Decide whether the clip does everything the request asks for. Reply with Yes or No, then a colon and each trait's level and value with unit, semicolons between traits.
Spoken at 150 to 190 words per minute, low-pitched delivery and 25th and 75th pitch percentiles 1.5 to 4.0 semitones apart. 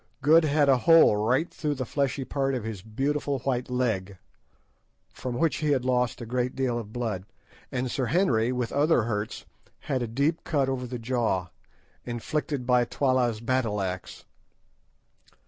Yes: average, 165 wpm; low, 125 Hz; average, 3.3 semitones